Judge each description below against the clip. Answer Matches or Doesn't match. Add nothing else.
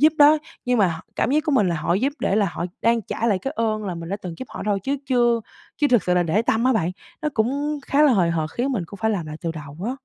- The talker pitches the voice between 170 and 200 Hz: Doesn't match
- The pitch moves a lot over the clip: Matches